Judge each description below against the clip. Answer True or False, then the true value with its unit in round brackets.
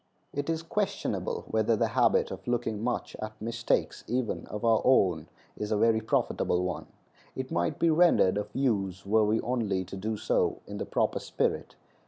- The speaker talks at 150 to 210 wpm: True (180 wpm)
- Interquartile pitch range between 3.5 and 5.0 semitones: True (3.9 semitones)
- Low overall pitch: True (110 Hz)